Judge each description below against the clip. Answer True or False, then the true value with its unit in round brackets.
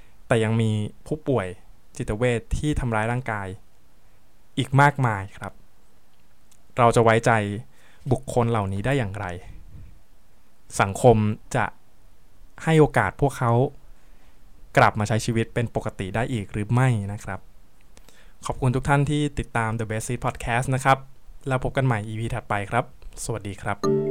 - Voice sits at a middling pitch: False (115 Hz)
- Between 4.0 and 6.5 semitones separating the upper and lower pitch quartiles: False (3.5 semitones)